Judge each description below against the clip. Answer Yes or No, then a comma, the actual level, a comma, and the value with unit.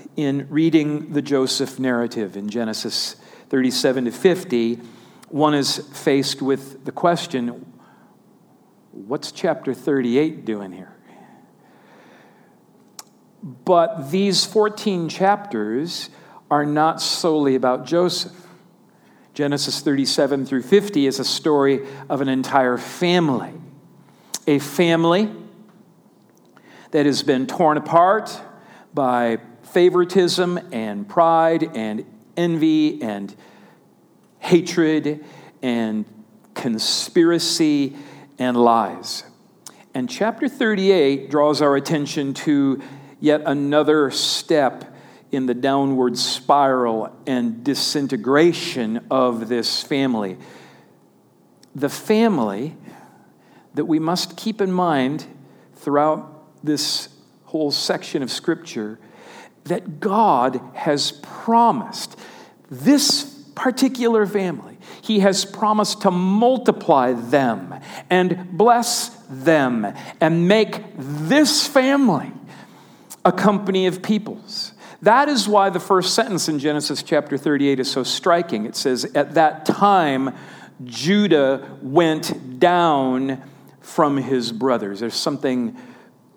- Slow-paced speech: Yes, slow, 100 wpm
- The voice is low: No, medium, 150 Hz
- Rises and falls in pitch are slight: No, wide, 5.5 semitones